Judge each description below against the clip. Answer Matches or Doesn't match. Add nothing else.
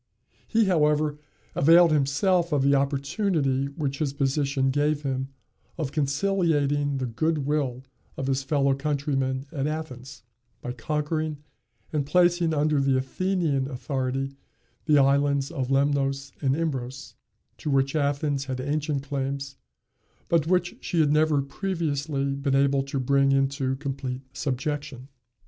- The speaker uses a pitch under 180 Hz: Matches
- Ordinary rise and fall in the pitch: Doesn't match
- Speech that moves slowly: Matches